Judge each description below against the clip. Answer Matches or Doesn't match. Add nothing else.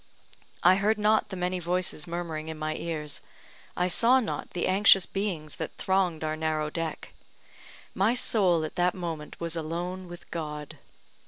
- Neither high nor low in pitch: Matches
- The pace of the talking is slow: Doesn't match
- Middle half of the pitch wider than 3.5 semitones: Doesn't match